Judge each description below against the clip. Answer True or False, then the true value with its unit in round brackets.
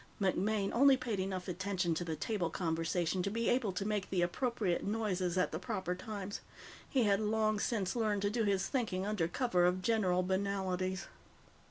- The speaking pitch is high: True (195 Hz)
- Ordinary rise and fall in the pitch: True (3.0 semitones)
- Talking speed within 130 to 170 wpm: False (180 wpm)